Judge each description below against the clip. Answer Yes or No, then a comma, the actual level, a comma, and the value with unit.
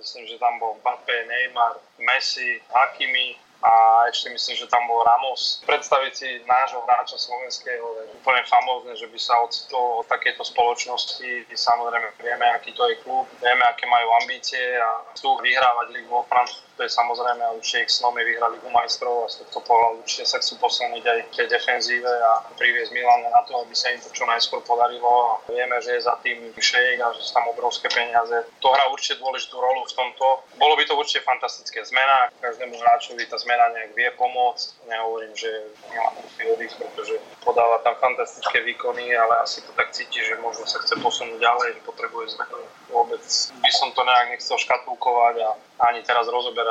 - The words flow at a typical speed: No, fast, 185 wpm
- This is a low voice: Yes, low, 120 Hz